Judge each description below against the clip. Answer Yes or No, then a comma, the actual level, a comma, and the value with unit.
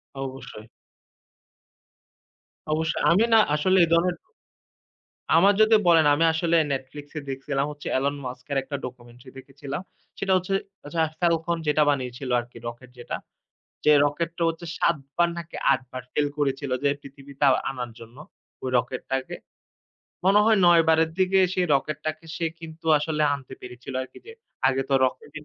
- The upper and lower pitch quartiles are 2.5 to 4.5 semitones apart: Yes, average, 4.2 semitones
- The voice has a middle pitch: Yes, medium, 145 Hz